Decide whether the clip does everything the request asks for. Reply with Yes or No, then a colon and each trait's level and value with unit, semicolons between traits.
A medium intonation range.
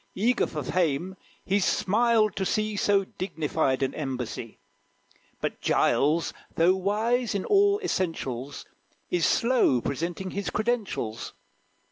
No: wide, 6.2 semitones